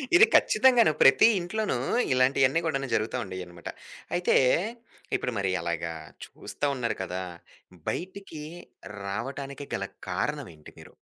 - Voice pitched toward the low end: Yes, low, 130 Hz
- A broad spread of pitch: Yes, wide, 8.8 semitones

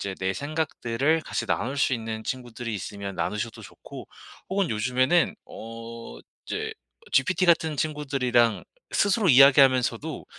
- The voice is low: Yes, low, 125 Hz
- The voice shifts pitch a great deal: No, average, 4.8 semitones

